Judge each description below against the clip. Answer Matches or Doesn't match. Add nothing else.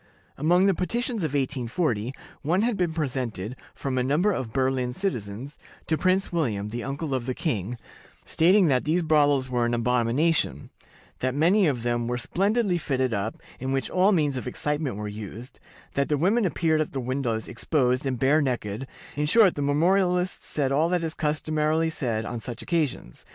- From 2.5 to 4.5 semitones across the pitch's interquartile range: Doesn't match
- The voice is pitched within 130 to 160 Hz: Matches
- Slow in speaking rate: Doesn't match